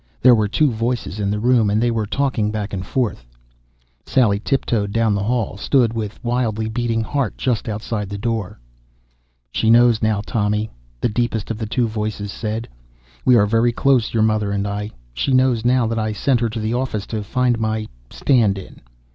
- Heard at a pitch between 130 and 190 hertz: No, low, 110 Hz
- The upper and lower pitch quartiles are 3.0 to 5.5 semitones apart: No, narrow, 2.4 semitones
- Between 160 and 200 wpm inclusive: Yes, average, 195 wpm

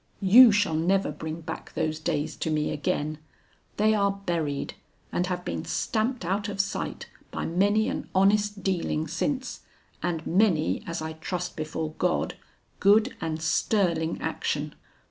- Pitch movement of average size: Yes, average, 4.2 semitones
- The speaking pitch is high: No, medium, 180 Hz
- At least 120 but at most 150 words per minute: Yes, average, 145 wpm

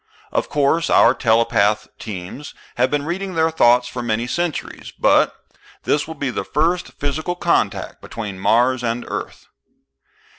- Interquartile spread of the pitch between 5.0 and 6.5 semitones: Yes, wide, 5.4 semitones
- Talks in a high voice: No, low, 130 Hz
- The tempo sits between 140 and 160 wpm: Yes, average, 145 wpm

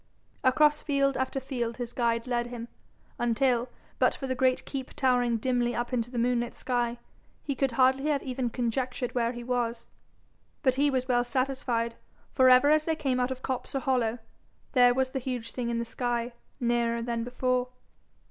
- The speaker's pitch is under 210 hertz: No, very high, 250 Hz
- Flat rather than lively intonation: Yes, narrow, 1.6 semitones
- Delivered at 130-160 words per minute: No, average, 185 wpm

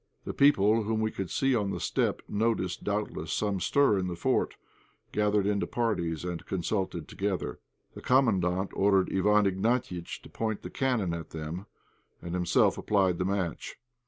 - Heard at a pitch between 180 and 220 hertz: No, low, 100 Hz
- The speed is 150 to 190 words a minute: Yes, average, 160 wpm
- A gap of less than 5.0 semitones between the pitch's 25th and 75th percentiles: Yes, average, 3.2 semitones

